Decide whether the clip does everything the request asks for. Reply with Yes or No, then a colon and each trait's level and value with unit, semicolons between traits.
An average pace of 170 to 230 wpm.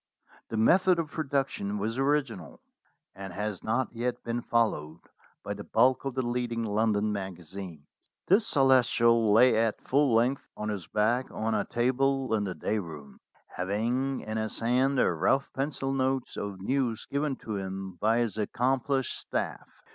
No: average, 160 wpm